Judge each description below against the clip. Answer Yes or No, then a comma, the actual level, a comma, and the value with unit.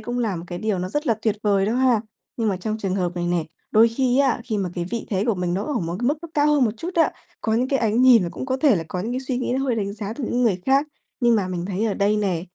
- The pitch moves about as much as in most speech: Yes, average, 4.9 semitones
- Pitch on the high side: Yes, high, 220 Hz